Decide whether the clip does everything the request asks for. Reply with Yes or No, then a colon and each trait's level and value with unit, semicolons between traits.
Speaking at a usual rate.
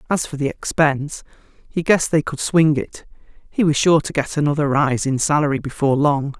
Yes: average, 195 wpm